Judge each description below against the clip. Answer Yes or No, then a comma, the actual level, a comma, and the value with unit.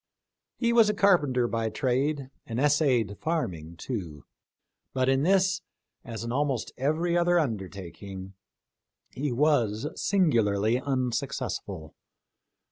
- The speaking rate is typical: No, slow, 110 wpm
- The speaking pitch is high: No, low, 130 Hz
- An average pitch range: No, wide, 6.1 semitones